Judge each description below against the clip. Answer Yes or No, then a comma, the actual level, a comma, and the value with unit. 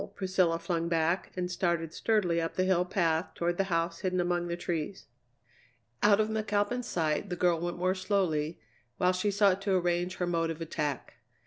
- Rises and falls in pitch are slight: Yes, narrow, 2.2 semitones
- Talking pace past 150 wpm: Yes, average, 185 wpm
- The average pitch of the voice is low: No, medium, 175 Hz